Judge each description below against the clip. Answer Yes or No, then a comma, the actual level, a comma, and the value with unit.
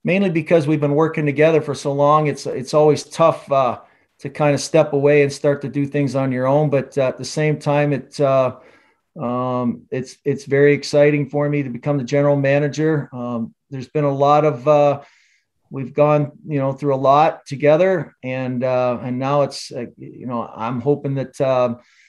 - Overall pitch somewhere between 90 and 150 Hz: Yes, medium, 140 Hz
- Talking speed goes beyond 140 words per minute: Yes, average, 200 wpm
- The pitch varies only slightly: Yes, narrow, 1.9 semitones